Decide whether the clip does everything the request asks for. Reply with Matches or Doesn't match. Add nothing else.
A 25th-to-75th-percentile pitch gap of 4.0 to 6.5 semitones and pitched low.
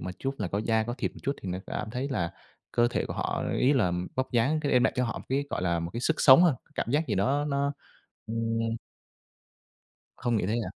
Matches